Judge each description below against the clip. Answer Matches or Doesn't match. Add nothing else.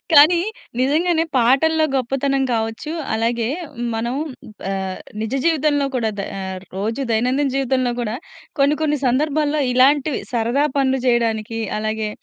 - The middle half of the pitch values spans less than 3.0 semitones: Doesn't match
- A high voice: Matches